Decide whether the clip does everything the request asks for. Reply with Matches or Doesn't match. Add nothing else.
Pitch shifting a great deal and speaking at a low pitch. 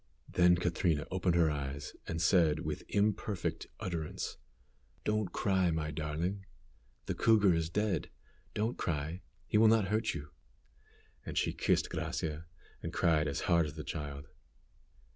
Doesn't match